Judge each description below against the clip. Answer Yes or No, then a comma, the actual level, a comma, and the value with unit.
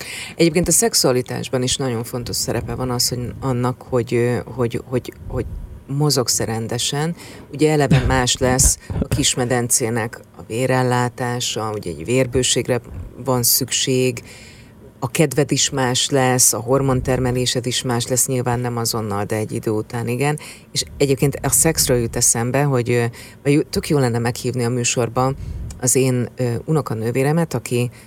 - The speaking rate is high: No, average, 140 wpm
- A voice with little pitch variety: Yes, narrow, 1.9 semitones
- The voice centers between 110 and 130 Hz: Yes, low, 125 Hz